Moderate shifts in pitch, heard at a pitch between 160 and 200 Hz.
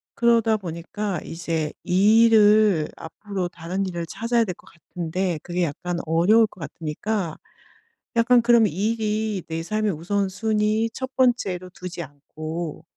Yes: average, 4.4 semitones; high, 190 Hz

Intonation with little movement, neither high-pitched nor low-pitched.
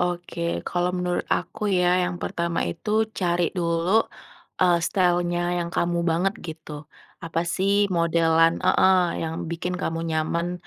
Yes: narrow, 1.3 semitones; medium, 175 Hz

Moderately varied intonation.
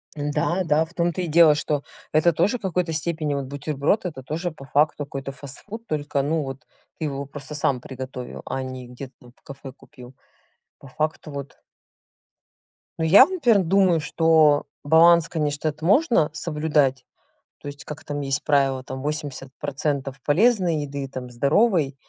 Yes: average, 3.2 semitones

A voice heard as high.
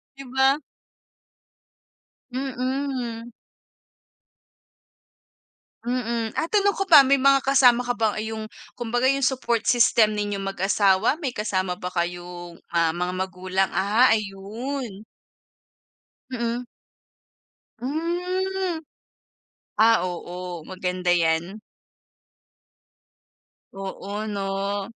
Yes: high, 220 Hz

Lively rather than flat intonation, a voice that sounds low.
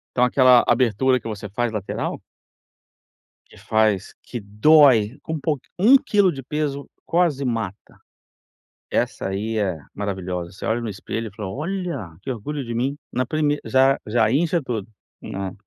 Yes: wide, 5.8 semitones; low, 120 Hz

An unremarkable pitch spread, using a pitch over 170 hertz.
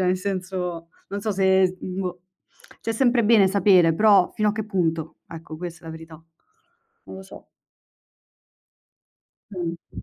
Yes: average, 3.0 semitones; medium, 185 Hz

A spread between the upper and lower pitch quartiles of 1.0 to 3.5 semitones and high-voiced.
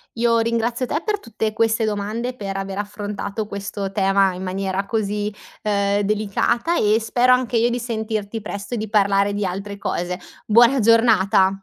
Yes: narrow, 2.5 semitones; high, 210 Hz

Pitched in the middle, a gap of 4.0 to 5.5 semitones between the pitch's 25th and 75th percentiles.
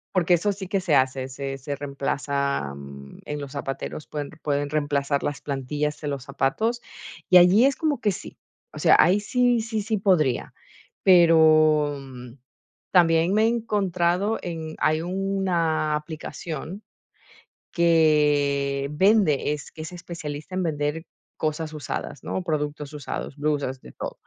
Yes: medium, 155 Hz; average, 4.4 semitones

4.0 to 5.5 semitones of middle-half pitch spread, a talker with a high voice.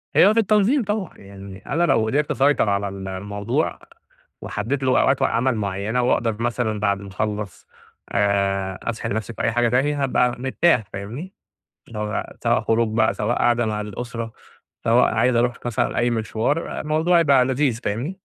No: average, 4.5 semitones; low, 115 Hz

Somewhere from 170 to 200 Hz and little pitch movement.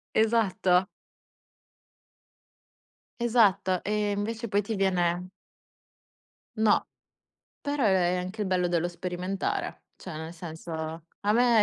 No: high, 190 Hz; average, 3.3 semitones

